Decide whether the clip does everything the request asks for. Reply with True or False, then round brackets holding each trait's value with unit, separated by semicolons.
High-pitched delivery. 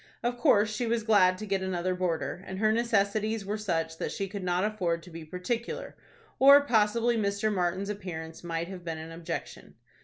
True (195 Hz)